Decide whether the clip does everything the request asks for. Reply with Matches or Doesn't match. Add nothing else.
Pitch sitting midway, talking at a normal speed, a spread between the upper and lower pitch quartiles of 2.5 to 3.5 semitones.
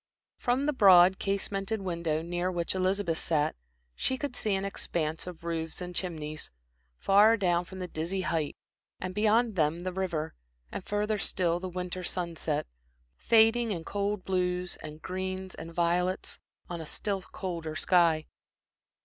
Matches